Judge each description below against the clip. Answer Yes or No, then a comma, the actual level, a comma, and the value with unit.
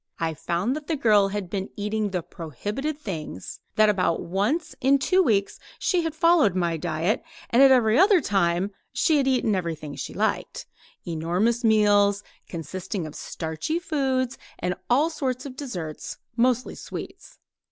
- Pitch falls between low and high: No, high, 210 Hz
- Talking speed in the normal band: Yes, average, 155 wpm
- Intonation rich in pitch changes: Yes, wide, 7.2 semitones